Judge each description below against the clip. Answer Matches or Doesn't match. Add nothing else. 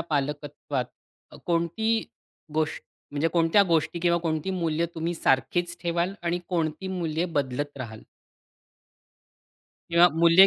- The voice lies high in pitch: Doesn't match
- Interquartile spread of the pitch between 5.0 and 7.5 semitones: Doesn't match